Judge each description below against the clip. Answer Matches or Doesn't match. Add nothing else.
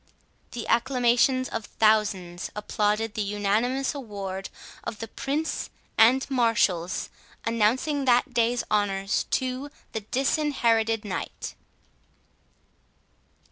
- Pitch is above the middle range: Matches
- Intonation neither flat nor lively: Matches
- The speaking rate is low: Matches